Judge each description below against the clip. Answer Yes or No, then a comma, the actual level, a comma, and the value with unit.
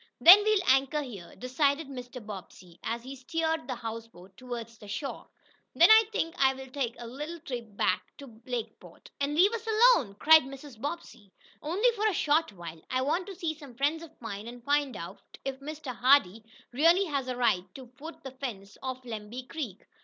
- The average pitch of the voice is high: Yes, very high, 265 Hz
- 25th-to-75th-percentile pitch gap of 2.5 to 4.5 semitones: No, average, 5.3 semitones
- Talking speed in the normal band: Yes, average, 180 wpm